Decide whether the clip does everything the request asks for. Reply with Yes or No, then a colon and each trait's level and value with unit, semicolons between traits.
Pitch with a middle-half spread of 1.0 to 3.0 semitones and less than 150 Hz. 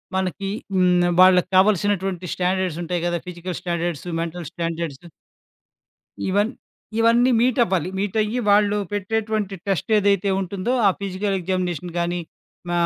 No: average, 2.7 semitones; medium, 185 Hz